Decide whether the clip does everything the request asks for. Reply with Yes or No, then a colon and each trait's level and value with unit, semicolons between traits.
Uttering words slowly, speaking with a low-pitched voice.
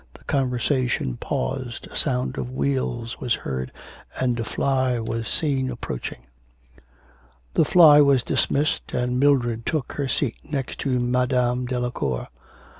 Yes: slow, 130 wpm; low, 125 Hz